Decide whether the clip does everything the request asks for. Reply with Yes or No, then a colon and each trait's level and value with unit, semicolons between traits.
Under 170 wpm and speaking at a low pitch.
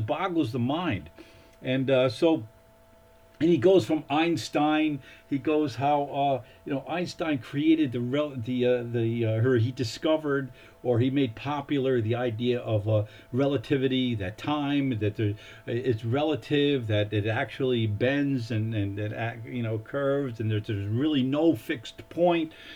Yes: average, 155 wpm; low, 130 Hz